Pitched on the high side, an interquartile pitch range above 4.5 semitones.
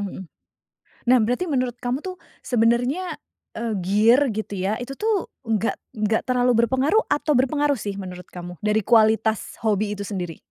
No: high, 230 Hz; average, 3.4 semitones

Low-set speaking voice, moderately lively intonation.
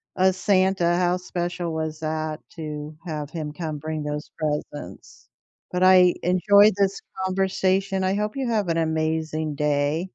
No: medium, 170 Hz; average, 3.2 semitones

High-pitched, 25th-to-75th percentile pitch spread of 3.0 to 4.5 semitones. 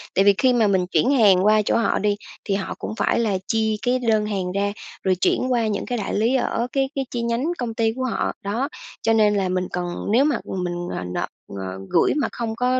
Yes: high, 220 Hz; average, 3.9 semitones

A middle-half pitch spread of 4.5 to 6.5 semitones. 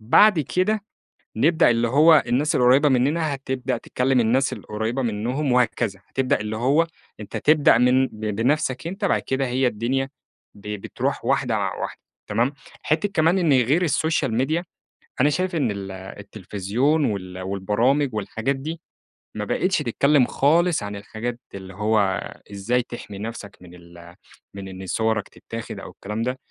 Yes: wide, 5.5 semitones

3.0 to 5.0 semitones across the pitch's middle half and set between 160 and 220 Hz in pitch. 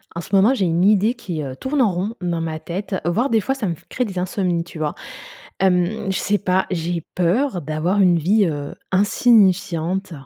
Yes: average, 3.4 semitones; medium, 185 Hz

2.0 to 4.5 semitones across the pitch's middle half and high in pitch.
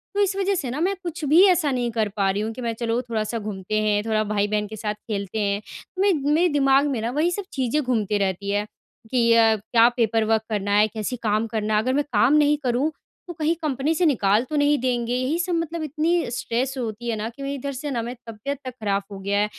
No: wide, 5.4 semitones; high, 235 Hz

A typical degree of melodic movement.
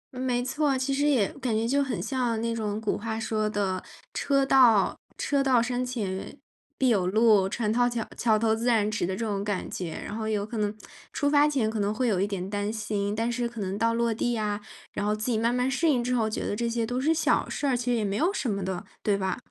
Yes: average, 3.2 semitones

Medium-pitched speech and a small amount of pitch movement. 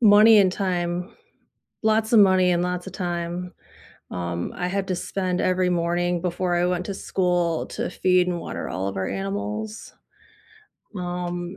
Yes: medium, 180 Hz; narrow, 1.4 semitones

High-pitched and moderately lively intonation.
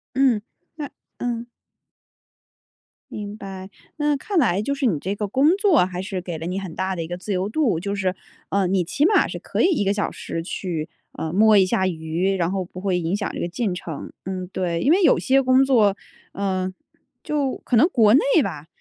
No: high, 195 Hz; wide, 5.9 semitones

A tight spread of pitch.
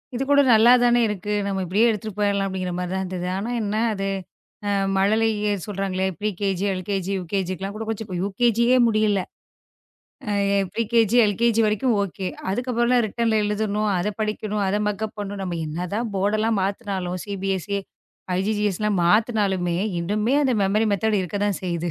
Yes: narrow, 2.3 semitones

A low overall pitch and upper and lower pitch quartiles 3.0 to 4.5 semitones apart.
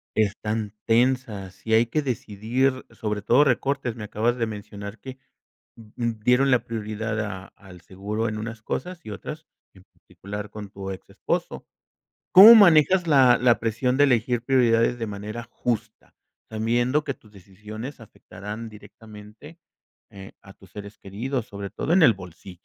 Yes: low, 110 Hz; average, 3.5 semitones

